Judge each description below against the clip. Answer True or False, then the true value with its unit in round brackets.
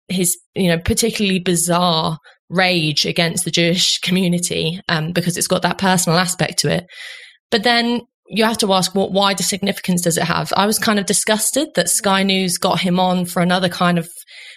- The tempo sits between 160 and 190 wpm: False (200 wpm)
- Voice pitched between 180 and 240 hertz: True (185 Hz)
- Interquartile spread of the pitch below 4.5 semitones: True (2.6 semitones)